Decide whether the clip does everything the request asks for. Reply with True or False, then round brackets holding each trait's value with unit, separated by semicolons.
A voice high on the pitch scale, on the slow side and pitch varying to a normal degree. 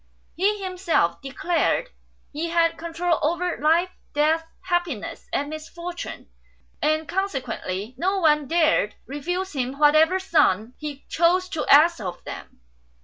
True (325 Hz; 125 wpm; 3.5 semitones)